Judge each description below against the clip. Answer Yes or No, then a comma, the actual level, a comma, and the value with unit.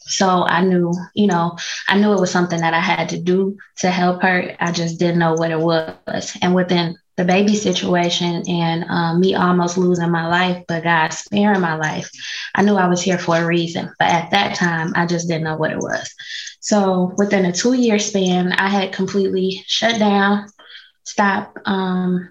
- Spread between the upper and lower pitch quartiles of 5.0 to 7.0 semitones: No, narrow, 2.4 semitones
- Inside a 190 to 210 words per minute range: Yes, average, 200 wpm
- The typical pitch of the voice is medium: Yes, medium, 180 Hz